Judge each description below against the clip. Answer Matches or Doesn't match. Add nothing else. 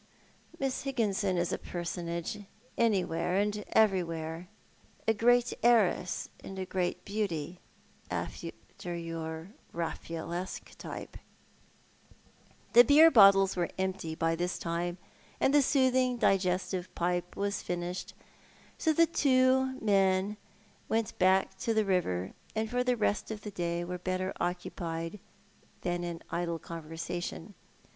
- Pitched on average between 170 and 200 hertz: Matches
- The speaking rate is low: Matches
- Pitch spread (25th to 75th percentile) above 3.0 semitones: Matches